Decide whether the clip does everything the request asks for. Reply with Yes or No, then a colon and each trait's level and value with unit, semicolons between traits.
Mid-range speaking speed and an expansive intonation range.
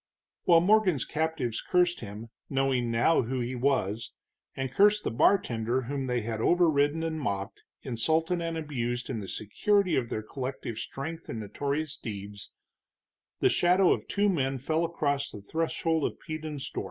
Yes: average, 160 wpm; wide, 5.7 semitones